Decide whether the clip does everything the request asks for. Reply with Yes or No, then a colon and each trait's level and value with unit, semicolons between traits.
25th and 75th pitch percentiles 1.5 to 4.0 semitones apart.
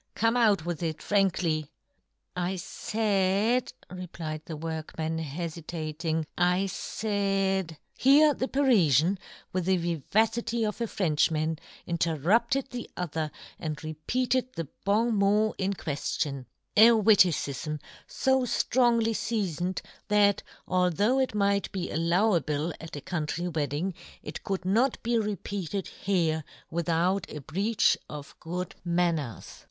No: average, 4.9 semitones